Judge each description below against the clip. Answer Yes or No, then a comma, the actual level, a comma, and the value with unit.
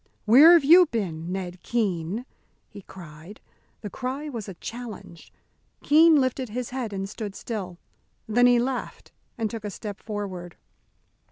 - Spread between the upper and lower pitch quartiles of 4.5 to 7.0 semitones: Yes, average, 4.8 semitones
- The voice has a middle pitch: No, high, 220 Hz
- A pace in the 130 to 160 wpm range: Yes, average, 150 wpm